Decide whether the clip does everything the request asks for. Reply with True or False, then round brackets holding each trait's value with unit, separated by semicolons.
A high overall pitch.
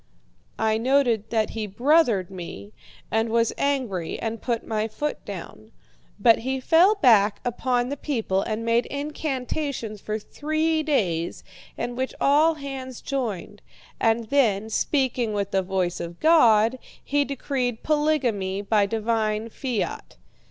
True (230 Hz)